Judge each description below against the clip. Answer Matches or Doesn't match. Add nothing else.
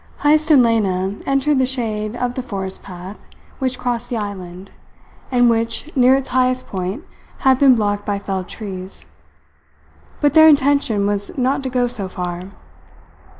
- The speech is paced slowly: Doesn't match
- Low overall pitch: Doesn't match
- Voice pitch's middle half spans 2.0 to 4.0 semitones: Doesn't match